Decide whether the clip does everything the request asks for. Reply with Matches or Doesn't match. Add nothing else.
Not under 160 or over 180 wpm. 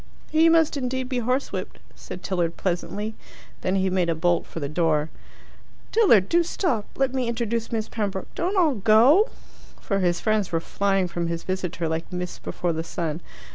Matches